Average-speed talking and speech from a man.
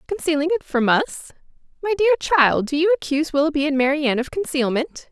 No: average, 175 wpm; female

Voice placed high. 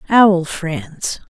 No: medium, 175 Hz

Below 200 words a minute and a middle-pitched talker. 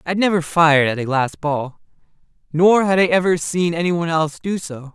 No: fast, 205 wpm; medium, 165 Hz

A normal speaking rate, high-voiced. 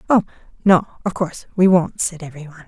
No: average, 180 wpm; medium, 175 Hz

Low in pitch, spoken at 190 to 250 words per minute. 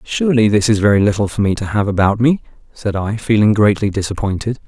Yes: low, 105 Hz; fast, 205 wpm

